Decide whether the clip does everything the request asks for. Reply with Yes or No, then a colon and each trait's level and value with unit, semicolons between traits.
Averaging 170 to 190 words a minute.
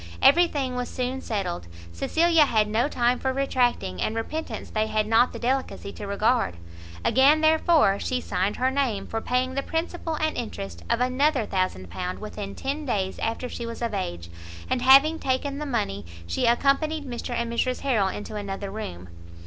Yes: average, 175 wpm